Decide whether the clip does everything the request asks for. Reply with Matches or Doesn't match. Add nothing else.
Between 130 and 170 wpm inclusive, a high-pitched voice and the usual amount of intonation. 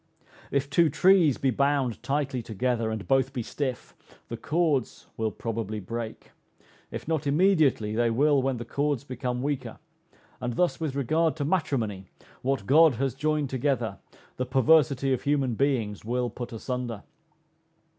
Doesn't match